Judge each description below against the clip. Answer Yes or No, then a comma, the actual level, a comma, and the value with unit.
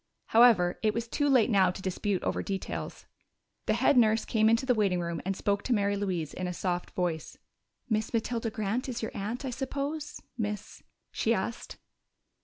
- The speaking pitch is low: No, high, 215 Hz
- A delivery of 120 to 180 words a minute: No, average, 190 wpm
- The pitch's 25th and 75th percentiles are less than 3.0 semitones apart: No, average, 3.8 semitones